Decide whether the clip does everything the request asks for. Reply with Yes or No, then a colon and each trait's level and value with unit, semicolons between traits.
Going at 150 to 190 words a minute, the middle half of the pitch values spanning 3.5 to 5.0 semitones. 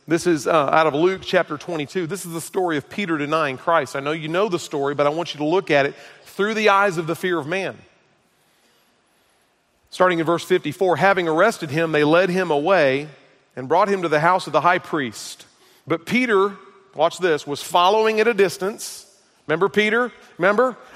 No: fast, 205 wpm; average, 4.3 semitones